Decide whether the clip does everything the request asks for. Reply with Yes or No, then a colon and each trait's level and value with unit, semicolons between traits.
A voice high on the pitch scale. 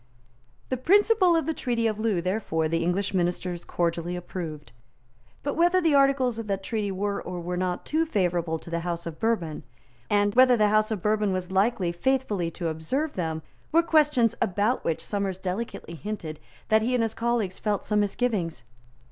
Yes: high, 205 Hz